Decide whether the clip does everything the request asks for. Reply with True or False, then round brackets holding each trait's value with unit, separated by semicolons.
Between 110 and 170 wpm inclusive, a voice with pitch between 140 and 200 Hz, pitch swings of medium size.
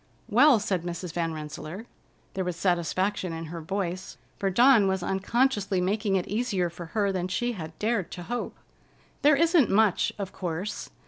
True (155 wpm; 190 Hz; 3.8 semitones)